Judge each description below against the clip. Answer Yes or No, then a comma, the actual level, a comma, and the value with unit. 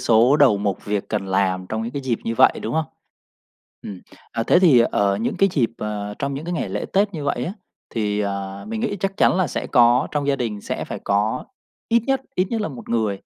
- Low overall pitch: Yes, low, 120 Hz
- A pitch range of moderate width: No, wide, 7.0 semitones